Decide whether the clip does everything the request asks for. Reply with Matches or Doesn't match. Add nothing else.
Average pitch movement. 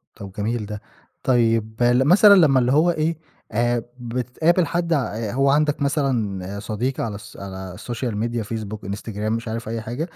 Matches